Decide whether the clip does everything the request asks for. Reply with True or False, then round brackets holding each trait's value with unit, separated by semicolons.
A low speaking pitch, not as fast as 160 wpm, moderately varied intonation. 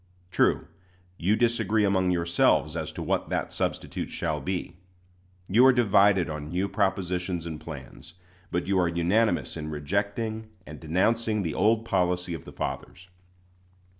True (95 Hz; 145 wpm; 3.6 semitones)